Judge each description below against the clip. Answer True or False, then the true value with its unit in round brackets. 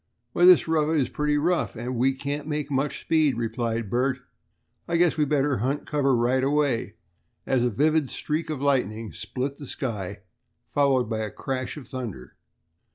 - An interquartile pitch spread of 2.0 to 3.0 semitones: False (3.6 semitones)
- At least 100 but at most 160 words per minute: False (170 wpm)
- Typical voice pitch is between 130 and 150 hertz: True (135 Hz)